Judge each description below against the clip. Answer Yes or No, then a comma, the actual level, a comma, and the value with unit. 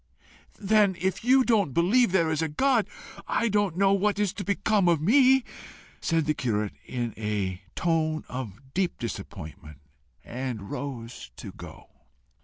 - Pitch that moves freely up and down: Yes, wide, 8.9 semitones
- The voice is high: No, medium, 165 Hz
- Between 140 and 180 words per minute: Yes, average, 150 wpm